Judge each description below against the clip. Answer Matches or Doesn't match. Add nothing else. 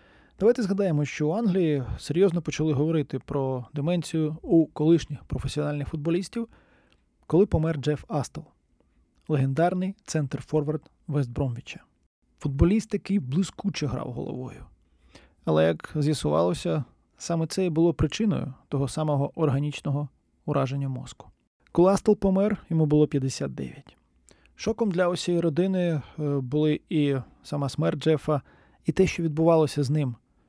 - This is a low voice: Doesn't match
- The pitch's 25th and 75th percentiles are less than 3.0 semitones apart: Doesn't match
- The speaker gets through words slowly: Doesn't match